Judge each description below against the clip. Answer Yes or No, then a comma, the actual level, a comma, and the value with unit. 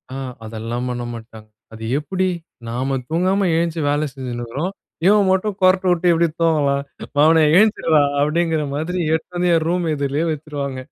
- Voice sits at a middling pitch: Yes, medium, 155 Hz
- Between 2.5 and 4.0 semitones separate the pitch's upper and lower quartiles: No, average, 4.5 semitones